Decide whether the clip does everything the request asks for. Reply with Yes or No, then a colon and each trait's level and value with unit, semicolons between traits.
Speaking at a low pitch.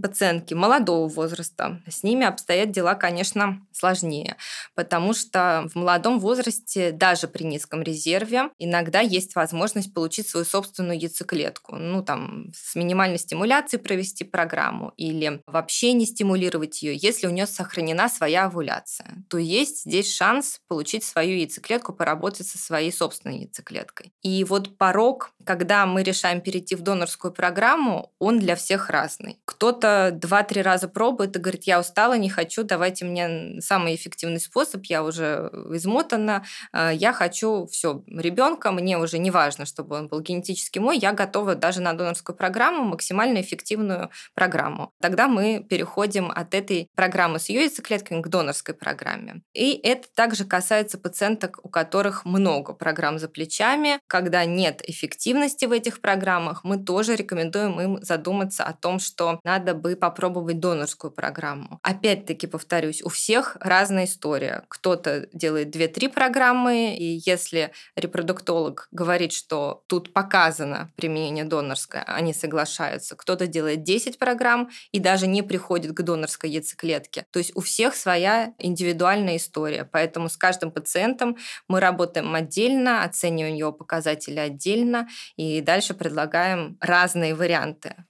No: medium, 180 Hz